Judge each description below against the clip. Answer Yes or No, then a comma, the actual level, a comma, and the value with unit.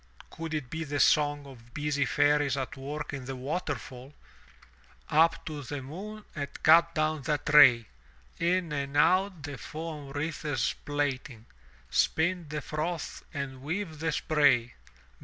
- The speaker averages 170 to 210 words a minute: No, average, 140 wpm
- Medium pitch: Yes, medium, 145 Hz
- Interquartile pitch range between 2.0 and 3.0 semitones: Yes, narrow, 2.6 semitones